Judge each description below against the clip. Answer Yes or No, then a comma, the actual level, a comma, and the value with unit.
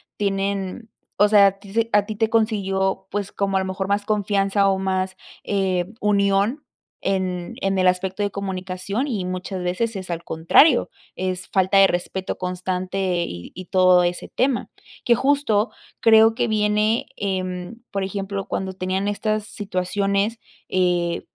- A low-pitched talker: No, high, 195 Hz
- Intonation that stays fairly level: Yes, narrow, 2.0 semitones